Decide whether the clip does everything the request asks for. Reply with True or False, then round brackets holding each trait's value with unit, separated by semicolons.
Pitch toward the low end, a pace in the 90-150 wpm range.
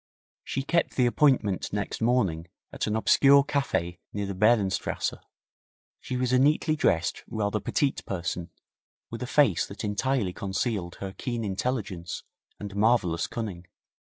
True (105 Hz; 140 wpm)